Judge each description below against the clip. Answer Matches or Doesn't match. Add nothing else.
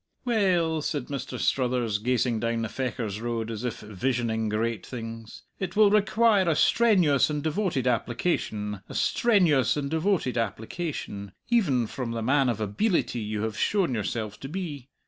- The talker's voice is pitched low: Matches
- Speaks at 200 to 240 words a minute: Doesn't match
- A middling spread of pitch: Doesn't match